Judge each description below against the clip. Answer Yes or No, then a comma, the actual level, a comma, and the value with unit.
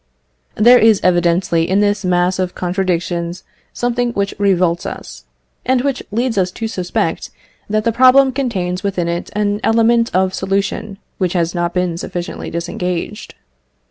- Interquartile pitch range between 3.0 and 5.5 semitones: Yes, average, 4.0 semitones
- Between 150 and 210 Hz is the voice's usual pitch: Yes, high, 190 Hz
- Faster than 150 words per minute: No, average, 145 wpm